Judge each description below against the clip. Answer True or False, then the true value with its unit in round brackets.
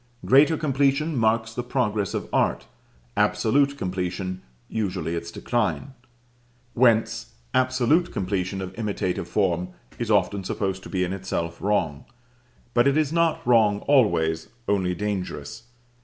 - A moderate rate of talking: False (125 wpm)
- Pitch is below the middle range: True (105 Hz)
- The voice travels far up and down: True (5.7 semitones)